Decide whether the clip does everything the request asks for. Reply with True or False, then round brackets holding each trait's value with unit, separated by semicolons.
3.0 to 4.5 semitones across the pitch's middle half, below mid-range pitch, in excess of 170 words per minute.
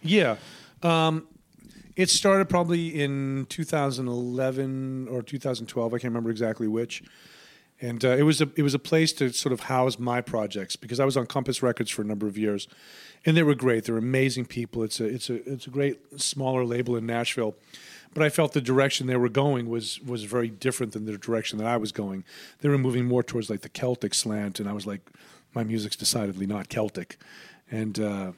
True (3.7 semitones; 125 Hz; 205 wpm)